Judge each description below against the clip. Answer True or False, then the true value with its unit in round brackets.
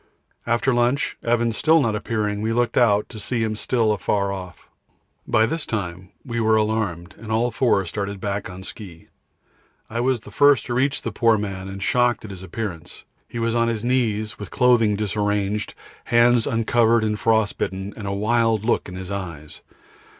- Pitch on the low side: True (110 Hz)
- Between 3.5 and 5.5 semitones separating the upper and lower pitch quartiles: False (3.0 semitones)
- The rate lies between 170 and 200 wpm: True (180 wpm)